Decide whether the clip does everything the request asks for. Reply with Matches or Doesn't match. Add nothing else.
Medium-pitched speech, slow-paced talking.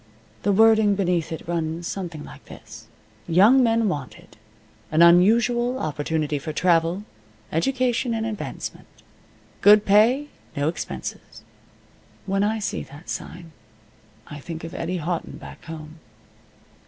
Matches